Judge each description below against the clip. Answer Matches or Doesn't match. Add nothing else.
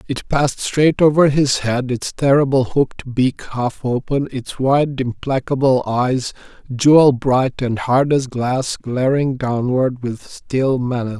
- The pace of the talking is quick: Doesn't match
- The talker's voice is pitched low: Matches